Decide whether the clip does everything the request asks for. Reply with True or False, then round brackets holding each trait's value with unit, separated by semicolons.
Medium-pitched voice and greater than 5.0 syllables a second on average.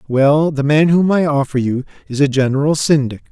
True (145 Hz; 5.2 syllables/s)